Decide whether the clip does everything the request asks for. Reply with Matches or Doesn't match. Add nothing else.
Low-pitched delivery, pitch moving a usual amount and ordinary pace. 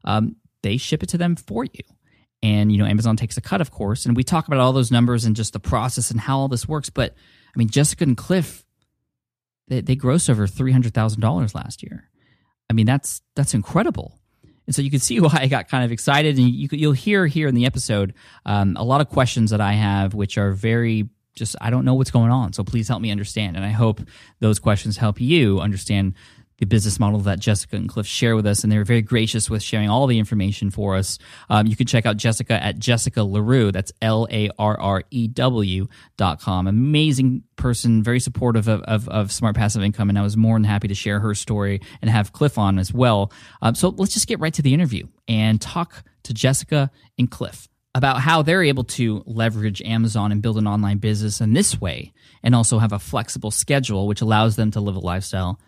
Doesn't match